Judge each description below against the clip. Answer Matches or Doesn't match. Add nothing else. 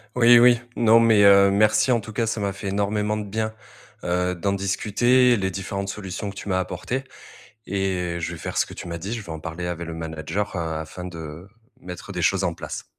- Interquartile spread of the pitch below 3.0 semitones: Doesn't match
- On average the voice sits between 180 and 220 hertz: Doesn't match